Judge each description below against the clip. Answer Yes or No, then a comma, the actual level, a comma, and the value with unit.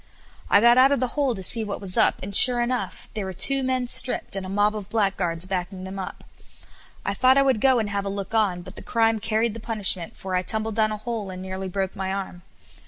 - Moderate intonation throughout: Yes, average, 3.5 semitones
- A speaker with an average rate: No, fast, 250 wpm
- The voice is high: Yes, high, 210 Hz